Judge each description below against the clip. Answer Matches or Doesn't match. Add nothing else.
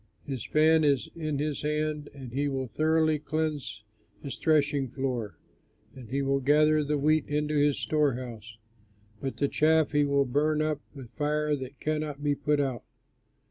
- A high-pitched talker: Doesn't match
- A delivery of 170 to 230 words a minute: Doesn't match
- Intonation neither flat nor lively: Doesn't match